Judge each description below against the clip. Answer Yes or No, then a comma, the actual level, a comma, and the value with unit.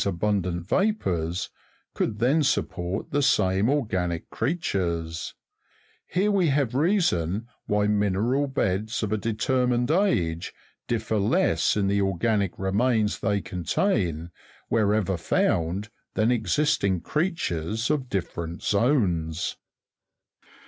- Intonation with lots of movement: Yes, wide, 6.0 semitones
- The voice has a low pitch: Yes, low, 105 Hz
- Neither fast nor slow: No, slow, 105 wpm